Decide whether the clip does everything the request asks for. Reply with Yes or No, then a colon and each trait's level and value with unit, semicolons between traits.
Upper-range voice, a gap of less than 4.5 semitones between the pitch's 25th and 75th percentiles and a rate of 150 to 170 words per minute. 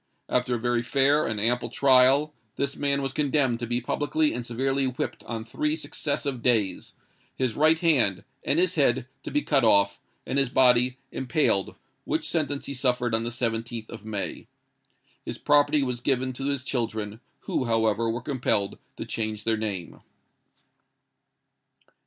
No: low, 125 Hz; average, 3.6 semitones; average, 160 wpm